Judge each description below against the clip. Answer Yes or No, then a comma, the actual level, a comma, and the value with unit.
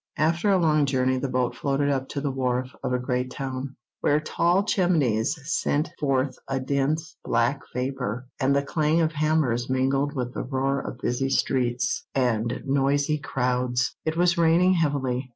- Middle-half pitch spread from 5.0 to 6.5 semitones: No, average, 3.0 semitones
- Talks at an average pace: Yes, average, 170 wpm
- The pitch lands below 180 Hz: Yes, low, 135 Hz